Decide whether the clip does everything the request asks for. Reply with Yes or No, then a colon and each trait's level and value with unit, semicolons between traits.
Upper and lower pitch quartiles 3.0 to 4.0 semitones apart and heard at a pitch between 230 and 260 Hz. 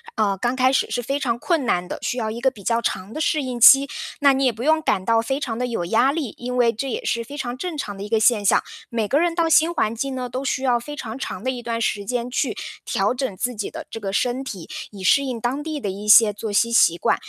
Yes: average, 3.7 semitones; high, 240 Hz